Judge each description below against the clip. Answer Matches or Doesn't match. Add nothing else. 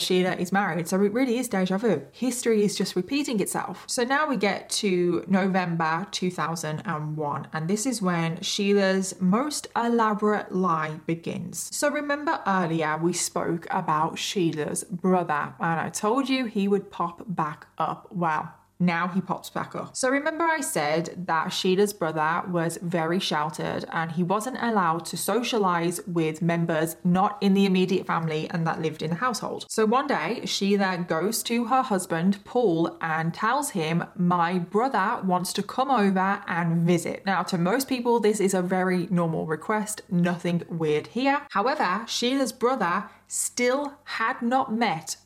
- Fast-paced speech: Doesn't match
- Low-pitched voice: Doesn't match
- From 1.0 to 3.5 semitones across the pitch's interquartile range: Doesn't match